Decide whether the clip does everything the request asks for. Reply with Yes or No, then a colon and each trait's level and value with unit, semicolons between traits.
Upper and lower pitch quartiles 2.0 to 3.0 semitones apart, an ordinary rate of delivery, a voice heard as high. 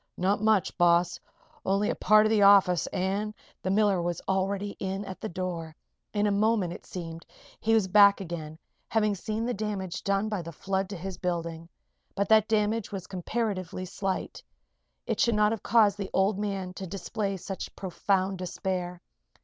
Yes: narrow, 2.5 semitones; average, 180 wpm; high, 195 Hz